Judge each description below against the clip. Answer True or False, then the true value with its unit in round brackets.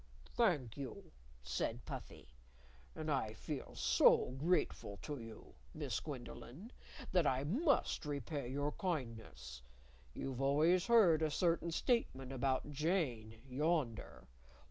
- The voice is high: False (140 Hz)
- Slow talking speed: True (115 wpm)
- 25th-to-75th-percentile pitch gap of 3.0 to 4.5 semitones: False (5.6 semitones)